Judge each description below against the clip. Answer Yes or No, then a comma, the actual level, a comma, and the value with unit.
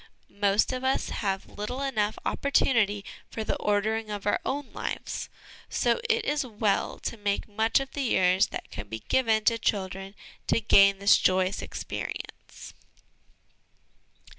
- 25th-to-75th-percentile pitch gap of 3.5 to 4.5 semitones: Yes, average, 3.9 semitones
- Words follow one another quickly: No, average, 145 wpm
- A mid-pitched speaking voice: No, high, 210 Hz